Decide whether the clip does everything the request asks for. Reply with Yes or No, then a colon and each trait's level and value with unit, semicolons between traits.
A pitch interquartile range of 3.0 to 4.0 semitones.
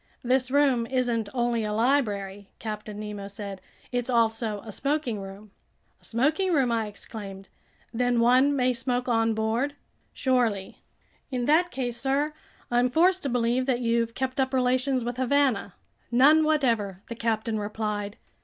Yes: average, 3.3 semitones